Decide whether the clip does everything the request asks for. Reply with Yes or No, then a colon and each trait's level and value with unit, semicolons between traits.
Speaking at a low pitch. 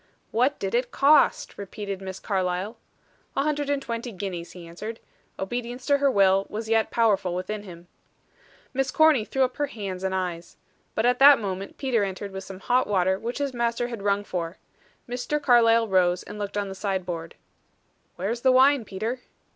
No: high, 210 Hz